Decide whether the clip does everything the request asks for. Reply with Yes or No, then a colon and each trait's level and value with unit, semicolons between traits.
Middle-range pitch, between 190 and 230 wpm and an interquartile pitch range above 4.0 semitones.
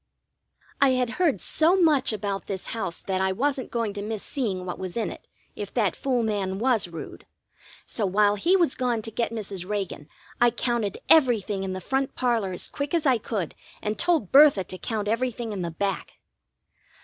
No: high, 220 Hz; average, 195 wpm; average, 4.7 semitones